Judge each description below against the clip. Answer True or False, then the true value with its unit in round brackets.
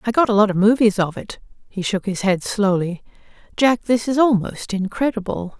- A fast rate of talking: False (195 wpm)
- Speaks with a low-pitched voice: False (215 Hz)